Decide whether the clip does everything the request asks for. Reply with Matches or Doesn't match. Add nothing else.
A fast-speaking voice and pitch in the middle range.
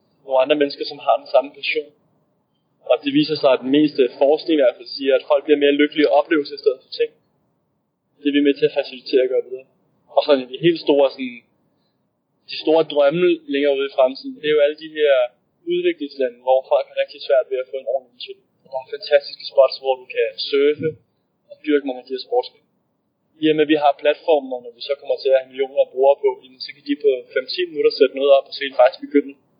Matches